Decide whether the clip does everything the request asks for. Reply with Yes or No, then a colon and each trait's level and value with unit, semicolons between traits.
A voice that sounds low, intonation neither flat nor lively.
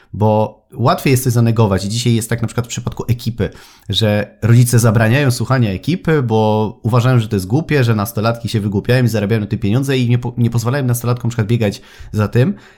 No: low, 115 Hz; narrow, 2.3 semitones